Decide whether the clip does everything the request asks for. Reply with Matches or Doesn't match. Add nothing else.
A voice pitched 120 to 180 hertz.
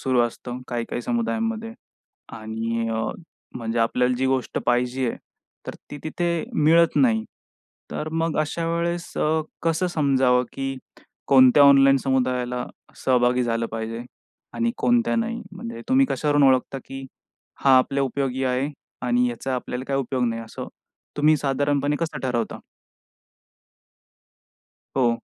Matches